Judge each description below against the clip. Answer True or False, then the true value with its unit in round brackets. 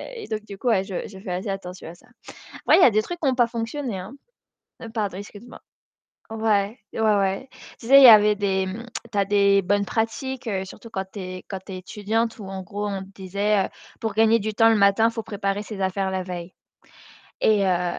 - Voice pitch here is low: False (205 Hz)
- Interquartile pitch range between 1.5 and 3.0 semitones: True (2.7 semitones)